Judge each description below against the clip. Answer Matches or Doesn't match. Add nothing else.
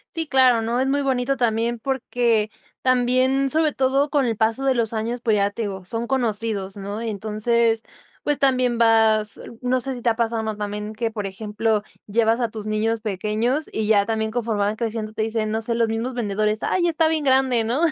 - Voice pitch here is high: Matches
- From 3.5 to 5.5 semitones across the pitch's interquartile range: Doesn't match